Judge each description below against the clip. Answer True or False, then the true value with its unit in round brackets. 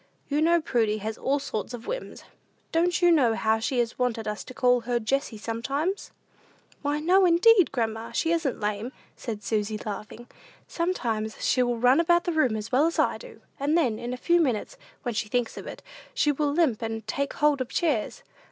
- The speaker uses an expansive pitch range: True (6.3 semitones)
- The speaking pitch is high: True (250 Hz)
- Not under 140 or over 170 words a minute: False (200 wpm)